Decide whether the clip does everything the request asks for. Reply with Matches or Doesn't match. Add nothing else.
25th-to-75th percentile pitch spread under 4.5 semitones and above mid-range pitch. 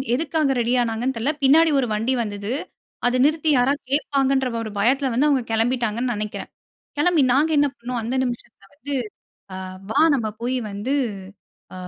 Matches